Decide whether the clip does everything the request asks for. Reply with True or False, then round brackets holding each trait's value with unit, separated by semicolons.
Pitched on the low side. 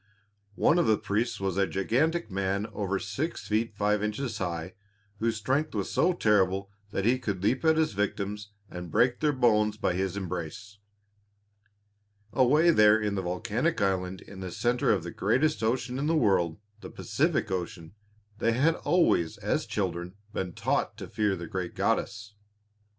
True (105 Hz)